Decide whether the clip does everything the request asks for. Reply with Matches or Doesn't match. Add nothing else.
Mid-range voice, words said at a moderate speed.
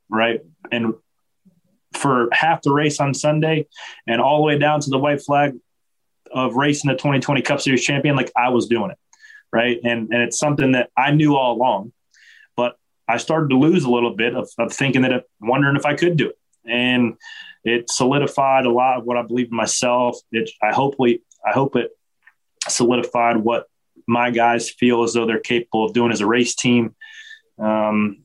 Doesn't match